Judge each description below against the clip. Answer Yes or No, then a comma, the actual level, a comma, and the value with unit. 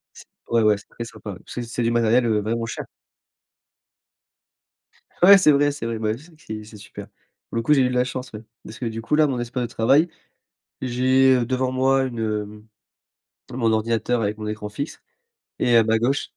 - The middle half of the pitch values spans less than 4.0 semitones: Yes, average, 2.9 semitones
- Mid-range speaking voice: No, low, 115 Hz